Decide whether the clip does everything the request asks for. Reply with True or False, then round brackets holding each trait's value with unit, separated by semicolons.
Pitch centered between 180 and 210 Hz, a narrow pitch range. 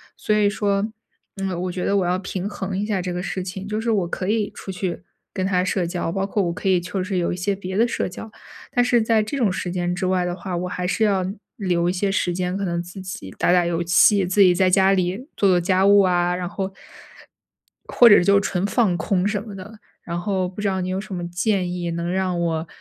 True (185 Hz; 2.1 semitones)